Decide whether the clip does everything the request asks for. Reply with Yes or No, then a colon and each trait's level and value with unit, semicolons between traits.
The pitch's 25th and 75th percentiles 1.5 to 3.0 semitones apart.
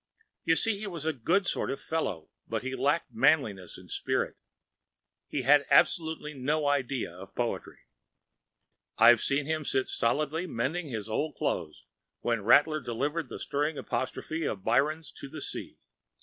No: average, 4.7 semitones